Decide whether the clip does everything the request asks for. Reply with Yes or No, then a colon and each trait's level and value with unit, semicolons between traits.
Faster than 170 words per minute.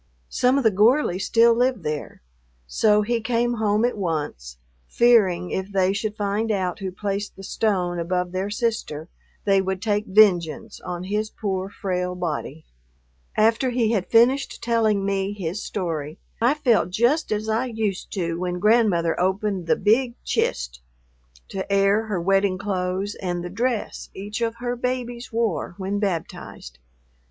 No: average, 155 wpm